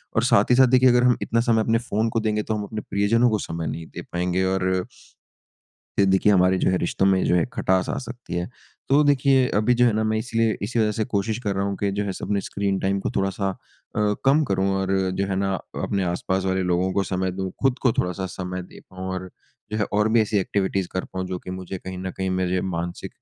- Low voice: Yes, low, 100 Hz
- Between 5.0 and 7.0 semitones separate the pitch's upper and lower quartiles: No, average, 2.9 semitones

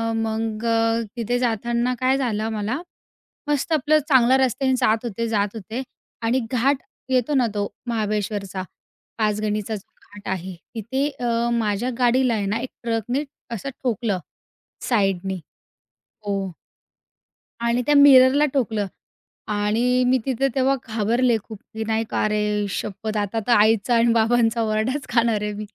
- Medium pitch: No, high, 225 Hz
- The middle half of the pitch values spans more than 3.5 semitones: No, average, 3.1 semitones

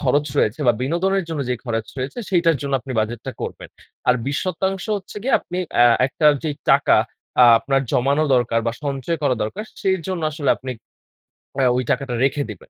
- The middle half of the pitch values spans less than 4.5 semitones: No, average, 5.1 semitones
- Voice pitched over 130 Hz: Yes, medium, 140 Hz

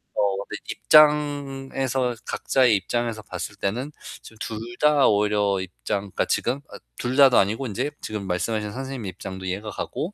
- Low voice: Yes, low, 115 Hz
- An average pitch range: Yes, average, 4.9 semitones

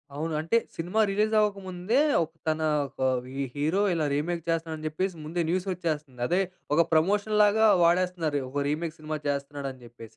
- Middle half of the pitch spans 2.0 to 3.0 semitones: No, average, 3.6 semitones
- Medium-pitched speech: Yes, medium, 165 Hz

